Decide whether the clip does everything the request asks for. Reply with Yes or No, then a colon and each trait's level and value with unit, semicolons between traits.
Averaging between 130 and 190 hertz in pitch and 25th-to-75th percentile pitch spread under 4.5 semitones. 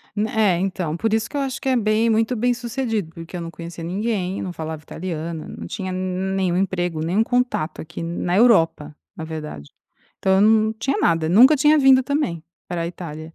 No: medium, 185 Hz; average, 5.1 semitones